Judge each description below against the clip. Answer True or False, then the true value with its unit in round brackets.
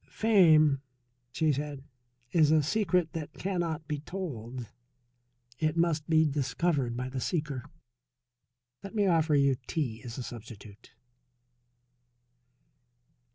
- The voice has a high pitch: False (150 Hz)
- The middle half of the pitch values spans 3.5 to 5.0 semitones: True (4.3 semitones)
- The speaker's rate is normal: False (110 wpm)